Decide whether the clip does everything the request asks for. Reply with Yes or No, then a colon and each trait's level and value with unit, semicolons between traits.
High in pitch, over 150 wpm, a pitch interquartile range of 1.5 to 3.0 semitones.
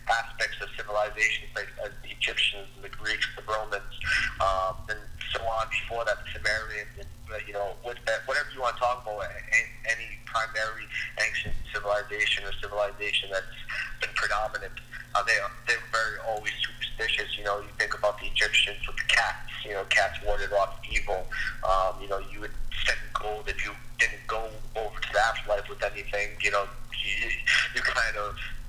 No: low, 110 Hz; average, 180 wpm; narrow, 2.5 semitones